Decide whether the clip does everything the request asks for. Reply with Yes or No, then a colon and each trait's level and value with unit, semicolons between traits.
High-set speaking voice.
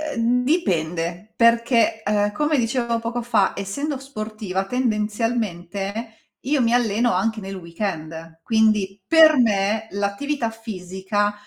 Yes: high, 220 Hz